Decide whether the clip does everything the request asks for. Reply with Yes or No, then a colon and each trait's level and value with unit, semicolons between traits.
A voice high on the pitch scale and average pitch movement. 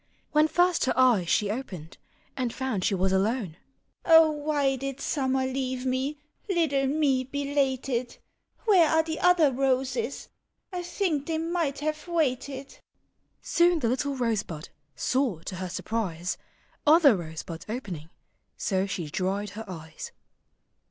No: very high, 265 Hz; wide, 6.7 semitones